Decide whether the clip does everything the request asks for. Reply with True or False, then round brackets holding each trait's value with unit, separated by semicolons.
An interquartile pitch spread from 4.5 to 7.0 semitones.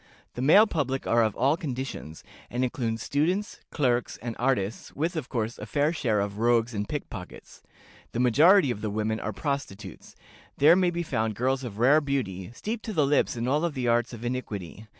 True (4.8 semitones)